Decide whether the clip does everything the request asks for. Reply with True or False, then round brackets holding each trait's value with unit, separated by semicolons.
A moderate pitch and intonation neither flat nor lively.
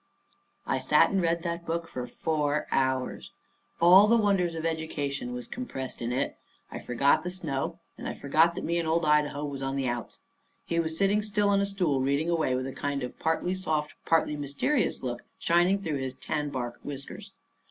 True (155 Hz; 3.9 semitones)